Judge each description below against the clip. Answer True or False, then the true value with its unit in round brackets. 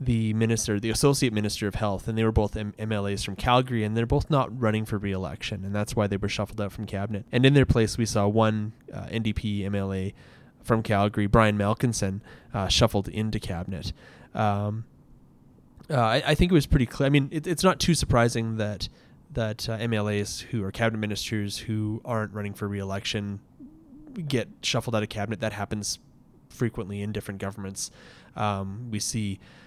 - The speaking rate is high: False (185 wpm)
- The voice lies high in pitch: False (110 Hz)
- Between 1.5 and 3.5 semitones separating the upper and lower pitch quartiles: True (2.4 semitones)